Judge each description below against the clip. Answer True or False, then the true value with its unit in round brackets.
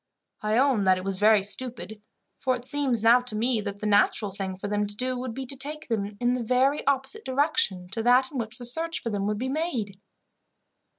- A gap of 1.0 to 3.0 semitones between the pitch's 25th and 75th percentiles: False (4.0 semitones)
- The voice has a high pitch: True (235 Hz)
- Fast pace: True (230 wpm)